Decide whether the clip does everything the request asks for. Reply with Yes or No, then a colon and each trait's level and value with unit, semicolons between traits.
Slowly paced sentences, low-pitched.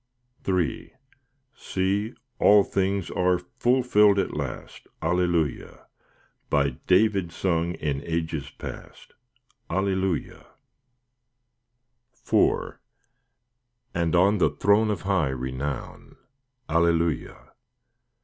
Yes: slow, 80 wpm; very low, 90 Hz